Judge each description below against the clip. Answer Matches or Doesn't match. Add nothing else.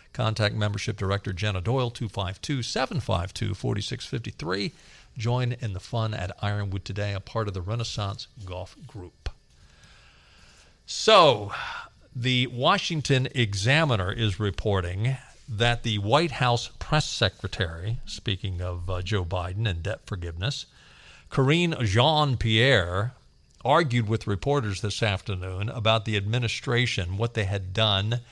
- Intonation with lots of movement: Doesn't match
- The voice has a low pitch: Matches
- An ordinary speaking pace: Doesn't match